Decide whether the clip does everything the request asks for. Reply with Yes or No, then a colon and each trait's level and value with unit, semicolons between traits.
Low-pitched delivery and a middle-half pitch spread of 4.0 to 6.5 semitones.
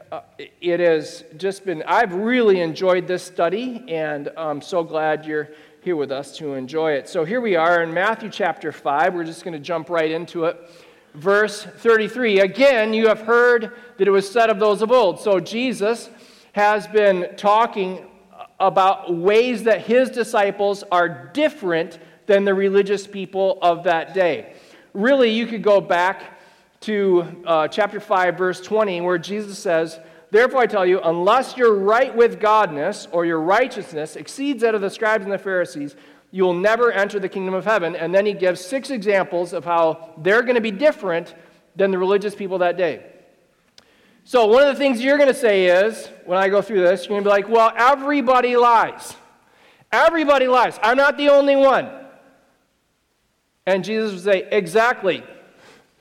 No: high, 195 Hz; average, 4.4 semitones